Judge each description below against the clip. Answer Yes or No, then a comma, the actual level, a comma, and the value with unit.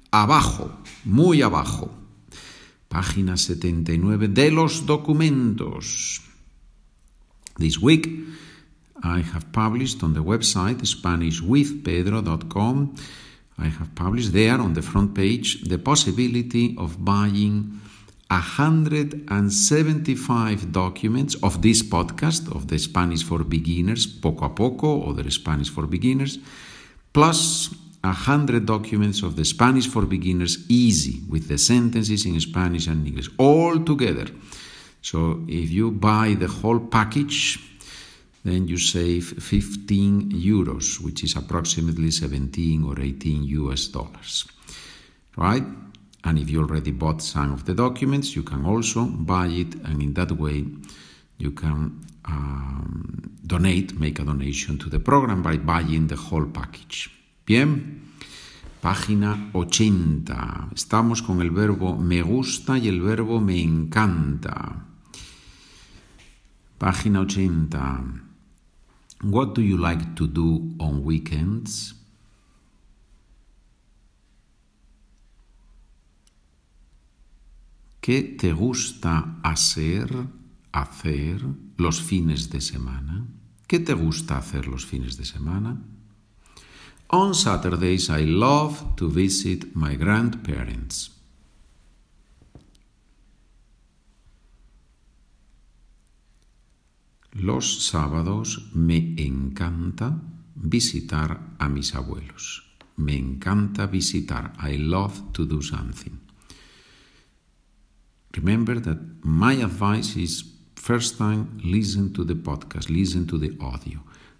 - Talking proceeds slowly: Yes, slow, 105 wpm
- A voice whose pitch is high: No, very low, 90 Hz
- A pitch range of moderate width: No, wide, 5.8 semitones